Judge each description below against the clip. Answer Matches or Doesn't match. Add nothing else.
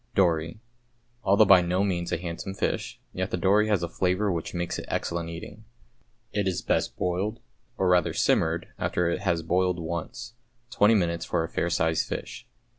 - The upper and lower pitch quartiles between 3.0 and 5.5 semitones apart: Doesn't match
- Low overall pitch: Matches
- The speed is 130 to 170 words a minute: Doesn't match